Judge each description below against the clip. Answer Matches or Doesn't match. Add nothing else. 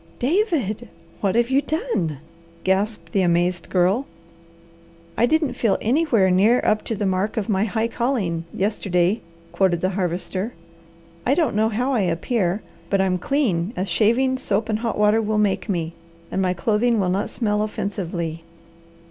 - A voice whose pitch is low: Doesn't match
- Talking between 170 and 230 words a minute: Doesn't match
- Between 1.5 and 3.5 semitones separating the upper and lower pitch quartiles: Doesn't match